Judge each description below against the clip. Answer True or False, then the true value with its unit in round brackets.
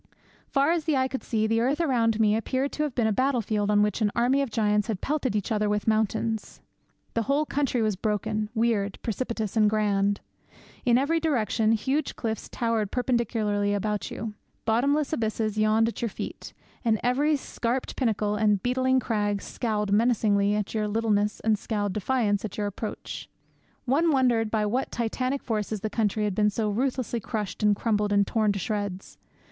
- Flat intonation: False (3.0 semitones)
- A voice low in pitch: False (220 Hz)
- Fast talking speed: False (185 wpm)